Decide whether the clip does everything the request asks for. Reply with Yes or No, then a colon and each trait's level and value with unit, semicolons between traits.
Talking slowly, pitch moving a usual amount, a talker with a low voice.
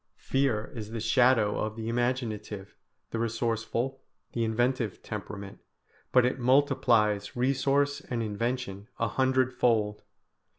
Yes: slow, 115 wpm; average, 3.2 semitones; low, 115 Hz